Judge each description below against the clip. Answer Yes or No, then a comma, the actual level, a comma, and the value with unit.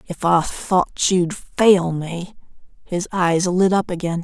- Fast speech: No, average, 155 wpm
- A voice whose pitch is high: No, medium, 180 Hz